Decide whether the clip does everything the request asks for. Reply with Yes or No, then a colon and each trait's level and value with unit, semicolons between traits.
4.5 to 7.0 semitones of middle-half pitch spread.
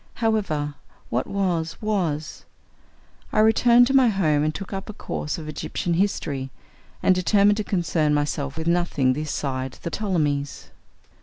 Yes: wide, 5.4 semitones